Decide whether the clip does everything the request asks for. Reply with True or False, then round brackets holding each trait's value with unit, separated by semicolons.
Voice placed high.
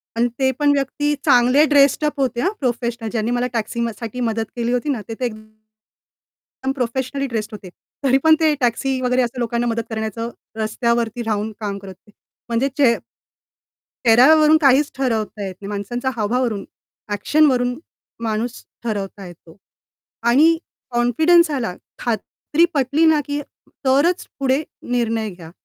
True (240 Hz)